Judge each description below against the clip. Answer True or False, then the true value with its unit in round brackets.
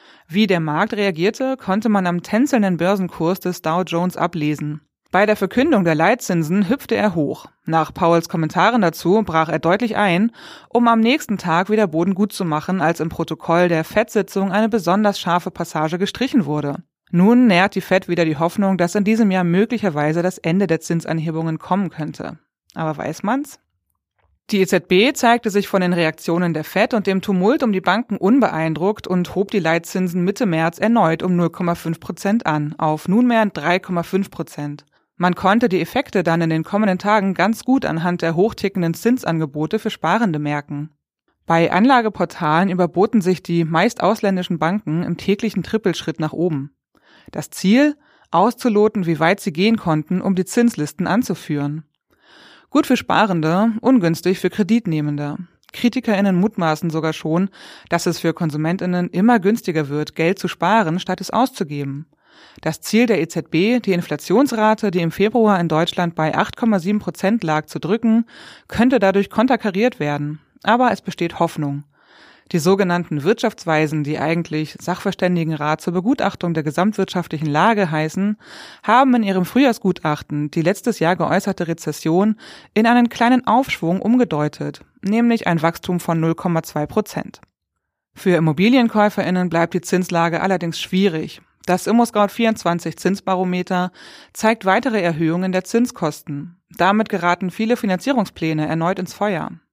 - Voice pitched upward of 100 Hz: True (185 Hz)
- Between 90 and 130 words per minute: False (145 wpm)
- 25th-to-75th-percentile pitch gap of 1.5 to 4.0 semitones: False (4.4 semitones)